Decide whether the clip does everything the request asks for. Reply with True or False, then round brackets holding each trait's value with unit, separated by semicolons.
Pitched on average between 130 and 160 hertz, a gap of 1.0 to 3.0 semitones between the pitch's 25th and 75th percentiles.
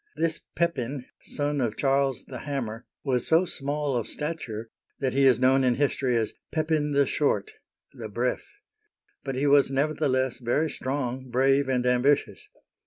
True (135 Hz; 2.6 semitones)